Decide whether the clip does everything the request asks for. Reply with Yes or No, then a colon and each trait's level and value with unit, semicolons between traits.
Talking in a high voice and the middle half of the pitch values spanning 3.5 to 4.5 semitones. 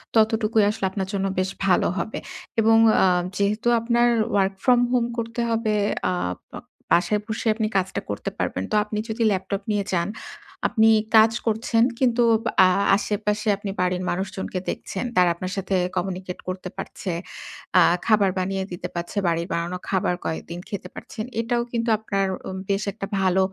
No: high, 200 Hz; average, 3.0 semitones